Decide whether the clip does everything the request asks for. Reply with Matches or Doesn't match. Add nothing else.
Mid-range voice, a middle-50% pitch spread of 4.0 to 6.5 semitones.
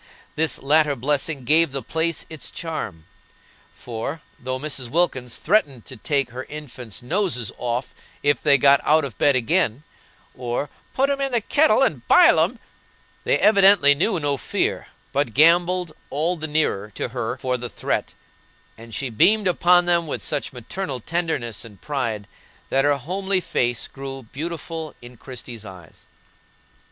Matches